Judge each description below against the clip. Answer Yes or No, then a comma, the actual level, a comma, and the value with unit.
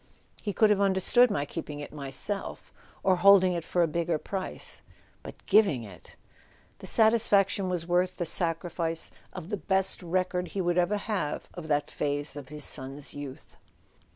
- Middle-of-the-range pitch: Yes, medium, 175 Hz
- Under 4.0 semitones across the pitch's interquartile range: No, average, 4.5 semitones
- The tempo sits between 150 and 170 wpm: Yes, average, 160 wpm